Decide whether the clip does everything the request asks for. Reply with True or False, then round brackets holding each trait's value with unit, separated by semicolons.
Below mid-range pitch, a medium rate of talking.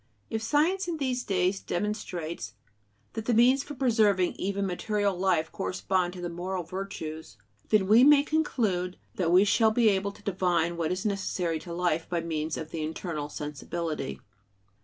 False (185 Hz; 160 wpm)